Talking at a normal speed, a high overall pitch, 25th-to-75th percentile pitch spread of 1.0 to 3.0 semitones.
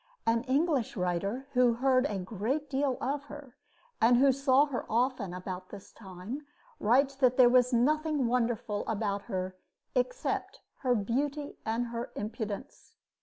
No: average, 145 wpm; high, 245 Hz; average, 4.4 semitones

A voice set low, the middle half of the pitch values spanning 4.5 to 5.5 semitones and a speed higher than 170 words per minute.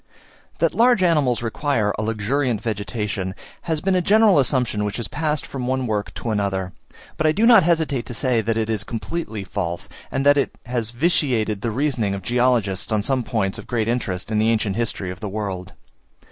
Yes: low, 115 Hz; average, 5.2 semitones; average, 200 wpm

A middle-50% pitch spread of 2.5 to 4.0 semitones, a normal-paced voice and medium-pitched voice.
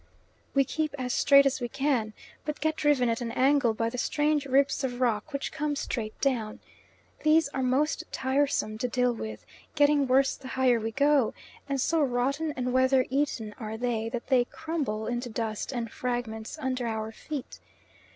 No: average, 3.4 semitones; average, 180 wpm; very high, 255 Hz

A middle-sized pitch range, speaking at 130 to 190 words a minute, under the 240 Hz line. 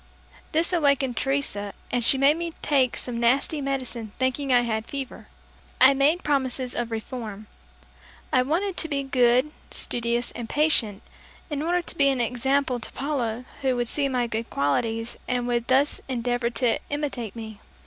No: average, 3.0 semitones; average, 165 wpm; very high, 255 Hz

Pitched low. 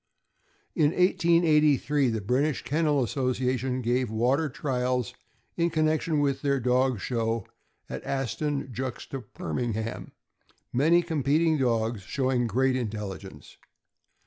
Yes: low, 130 Hz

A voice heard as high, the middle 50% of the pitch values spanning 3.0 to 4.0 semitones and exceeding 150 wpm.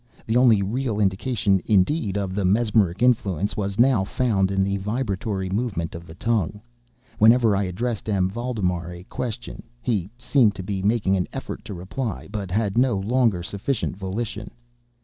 No: low, 100 Hz; average, 3.6 semitones; average, 165 wpm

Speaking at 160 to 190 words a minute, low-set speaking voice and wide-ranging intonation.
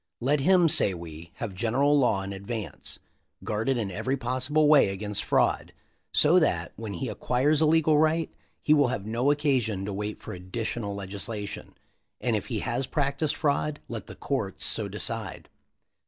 Yes: average, 170 wpm; low, 120 Hz; wide, 6.4 semitones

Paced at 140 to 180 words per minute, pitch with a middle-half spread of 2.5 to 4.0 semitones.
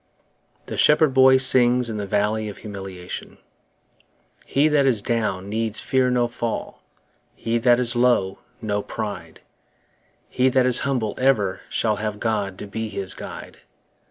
Yes: average, 150 wpm; average, 3.5 semitones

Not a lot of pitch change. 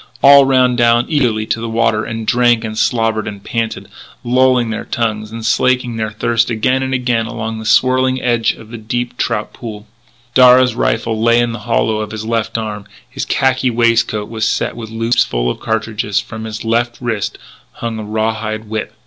Yes: narrow, 1.8 semitones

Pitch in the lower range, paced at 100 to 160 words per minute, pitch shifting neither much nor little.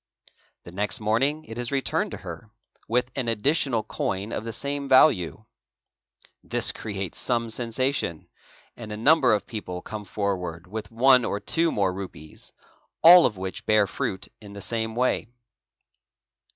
Yes: low, 110 Hz; average, 155 wpm; average, 4.3 semitones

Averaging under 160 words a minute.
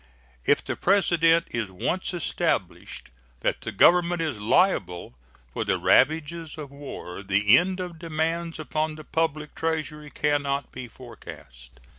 Yes: average, 140 wpm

